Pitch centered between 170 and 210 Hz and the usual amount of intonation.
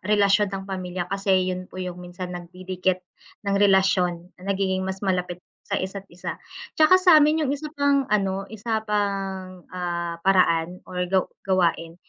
No: high, 190 Hz; narrow, 1.8 semitones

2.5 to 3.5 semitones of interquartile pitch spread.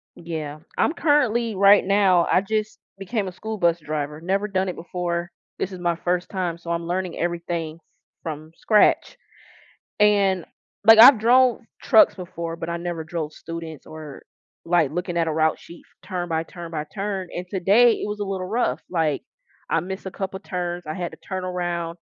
Yes: average, 2.9 semitones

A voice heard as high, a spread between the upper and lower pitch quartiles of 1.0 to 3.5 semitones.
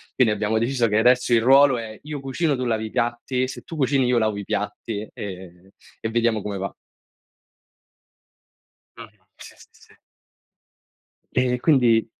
No: low, 120 Hz; average, 2.9 semitones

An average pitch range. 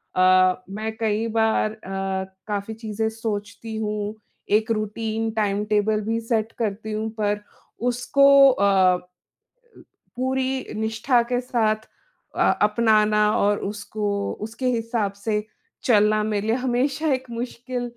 No: narrow, 1.9 semitones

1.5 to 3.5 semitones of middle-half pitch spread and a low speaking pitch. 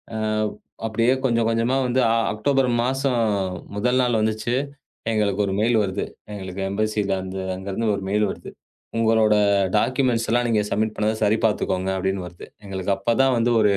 Yes: average, 3.0 semitones; low, 110 Hz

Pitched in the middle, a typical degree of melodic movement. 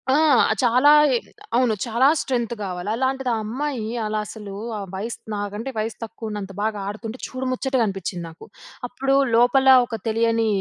No: high, 230 Hz; average, 3.3 semitones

